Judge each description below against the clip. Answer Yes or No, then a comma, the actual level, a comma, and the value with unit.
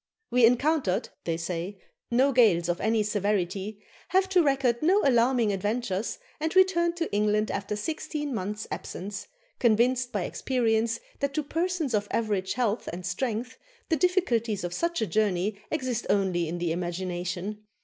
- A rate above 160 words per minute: No, average, 150 wpm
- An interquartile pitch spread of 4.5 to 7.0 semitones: Yes, wide, 5.4 semitones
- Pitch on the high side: Yes, high, 220 Hz